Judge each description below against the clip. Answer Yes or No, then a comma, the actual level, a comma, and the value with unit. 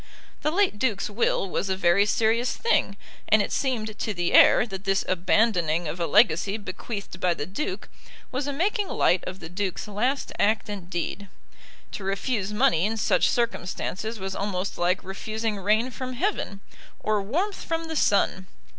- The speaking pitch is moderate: No, high, 205 Hz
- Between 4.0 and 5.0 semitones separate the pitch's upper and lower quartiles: Yes, average, 4.3 semitones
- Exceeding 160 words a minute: Yes, average, 170 wpm